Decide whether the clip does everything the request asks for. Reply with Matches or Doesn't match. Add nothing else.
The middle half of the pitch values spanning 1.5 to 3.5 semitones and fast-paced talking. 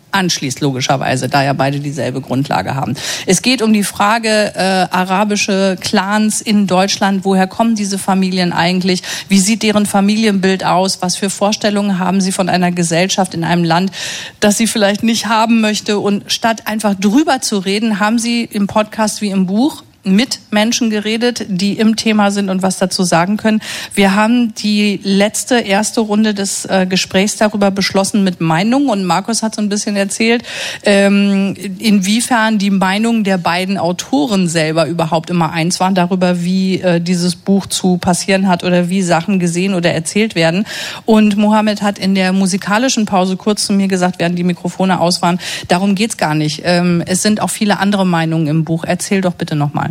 Doesn't match